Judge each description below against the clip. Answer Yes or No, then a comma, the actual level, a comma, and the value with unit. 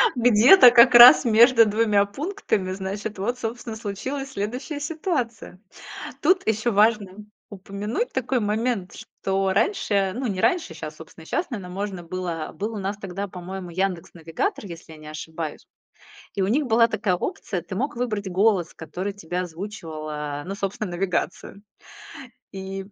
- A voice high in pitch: Yes, high, 200 Hz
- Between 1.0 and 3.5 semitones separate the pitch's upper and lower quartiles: No, average, 4.2 semitones